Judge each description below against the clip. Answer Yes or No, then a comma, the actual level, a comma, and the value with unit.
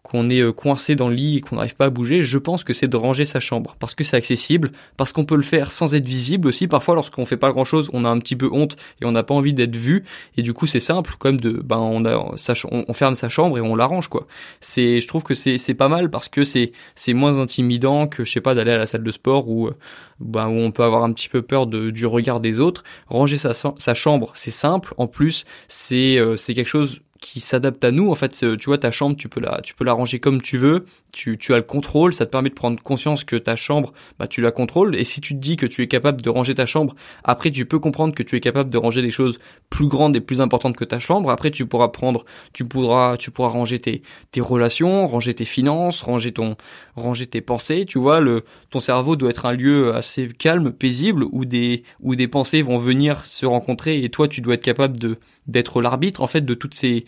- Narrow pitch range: No, average, 3.3 semitones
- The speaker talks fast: Yes, fast, 260 wpm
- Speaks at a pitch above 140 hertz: No, low, 130 Hz